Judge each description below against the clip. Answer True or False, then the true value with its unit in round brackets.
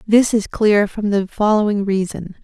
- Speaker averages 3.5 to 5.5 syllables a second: True (4.5 syllables/s)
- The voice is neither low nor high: False (205 Hz)